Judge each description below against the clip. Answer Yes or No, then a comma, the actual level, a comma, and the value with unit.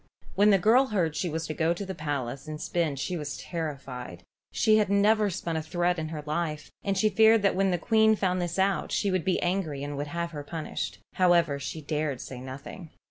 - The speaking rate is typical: No, fast, 225 wpm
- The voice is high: No, medium, 170 Hz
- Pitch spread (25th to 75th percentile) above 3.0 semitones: Yes, average, 4.3 semitones